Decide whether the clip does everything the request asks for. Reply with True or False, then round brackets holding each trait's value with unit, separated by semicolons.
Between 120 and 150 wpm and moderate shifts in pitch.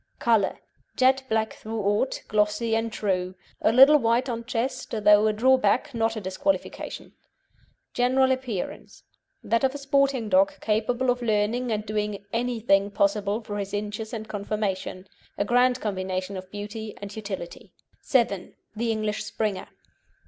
True (140 wpm; 3.0 semitones)